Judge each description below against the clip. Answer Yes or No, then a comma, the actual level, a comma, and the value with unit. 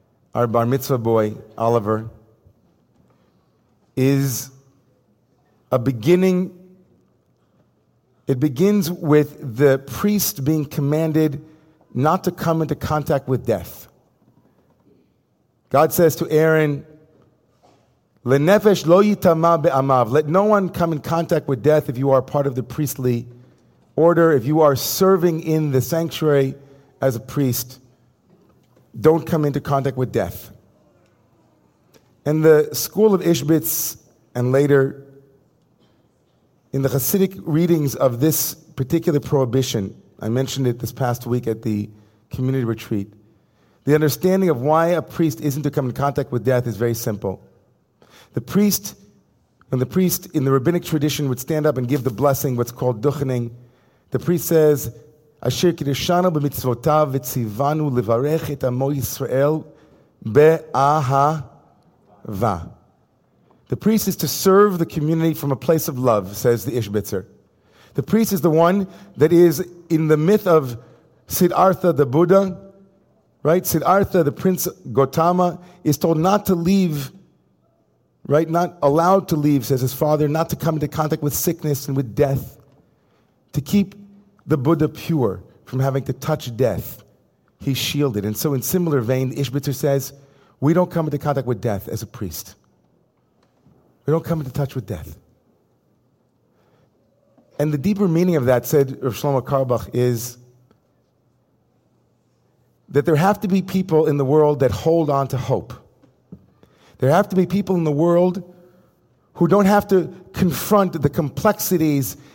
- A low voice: No, medium, 145 Hz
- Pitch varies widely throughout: No, average, 4.4 semitones